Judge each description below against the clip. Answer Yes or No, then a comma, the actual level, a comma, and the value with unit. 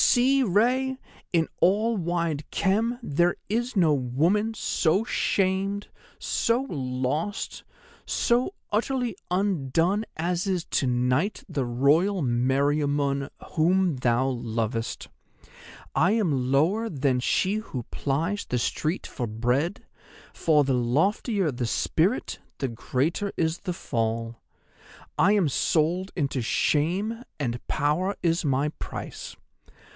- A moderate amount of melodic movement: No, wide, 7.1 semitones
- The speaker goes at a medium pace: No, slow, 115 wpm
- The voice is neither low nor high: Yes, medium, 165 Hz